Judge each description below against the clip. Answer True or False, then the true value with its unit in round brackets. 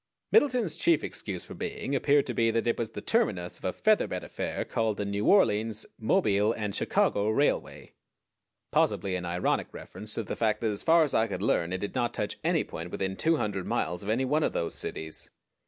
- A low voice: True (110 Hz)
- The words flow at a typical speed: False (210 wpm)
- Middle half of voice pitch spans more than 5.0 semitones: True (5.5 semitones)